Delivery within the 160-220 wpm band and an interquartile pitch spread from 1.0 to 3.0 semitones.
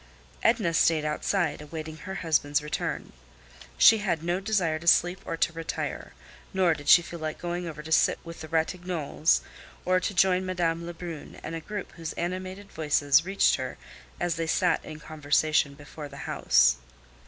Yes: average, 170 wpm; narrow, 2.5 semitones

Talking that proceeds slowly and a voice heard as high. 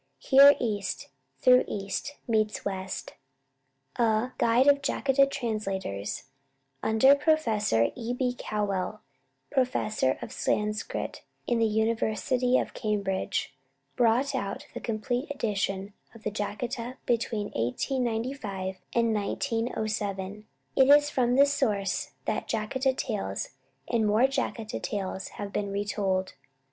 Yes: slow, 115 wpm; high, 220 Hz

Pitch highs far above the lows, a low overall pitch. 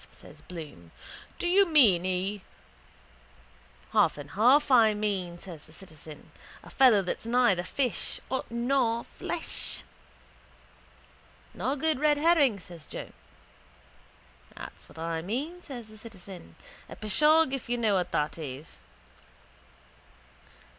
No: wide, 7.2 semitones; high, 215 Hz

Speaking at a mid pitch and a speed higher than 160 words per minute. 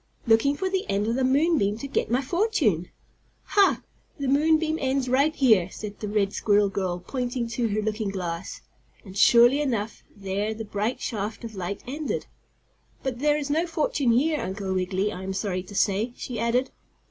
No: high, 230 Hz; average, 190 wpm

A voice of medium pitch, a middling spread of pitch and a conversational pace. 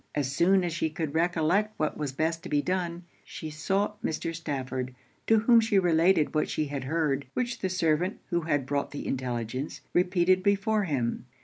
Yes: medium, 165 Hz; average, 4.4 semitones; average, 185 wpm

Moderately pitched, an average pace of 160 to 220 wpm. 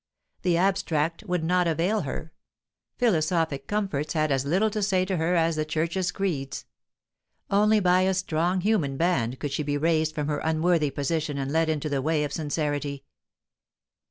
Yes: medium, 160 Hz; average, 170 wpm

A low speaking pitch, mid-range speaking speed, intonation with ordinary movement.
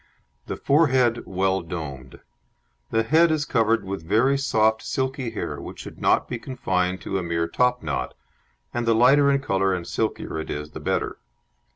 No: low, 115 Hz; average, 170 wpm; wide, 6.1 semitones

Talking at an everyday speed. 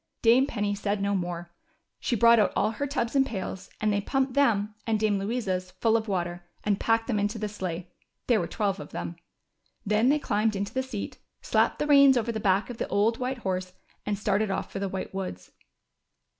No: fast, 215 wpm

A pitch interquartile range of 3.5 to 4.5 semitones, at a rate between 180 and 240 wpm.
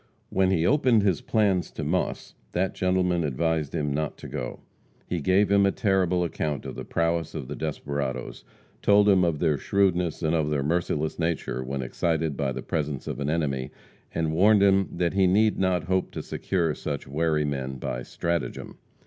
Yes: average, 4.2 semitones; average, 185 wpm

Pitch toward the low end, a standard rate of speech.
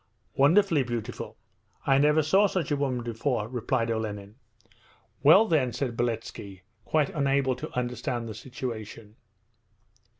No: low, 125 Hz; slow, 125 wpm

